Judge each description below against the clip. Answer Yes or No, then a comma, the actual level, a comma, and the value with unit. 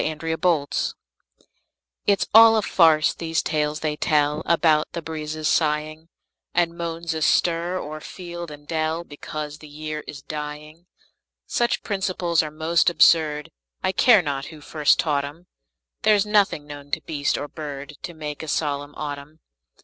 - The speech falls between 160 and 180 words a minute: No, average, 150 wpm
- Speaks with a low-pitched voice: No, medium, 155 Hz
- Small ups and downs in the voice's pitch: Yes, narrow, 2.2 semitones